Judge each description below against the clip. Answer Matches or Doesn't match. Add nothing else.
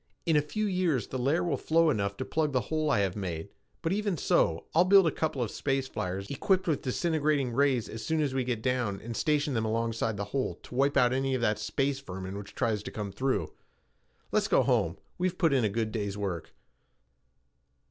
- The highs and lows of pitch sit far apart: Matches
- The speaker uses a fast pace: Matches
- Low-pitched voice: Matches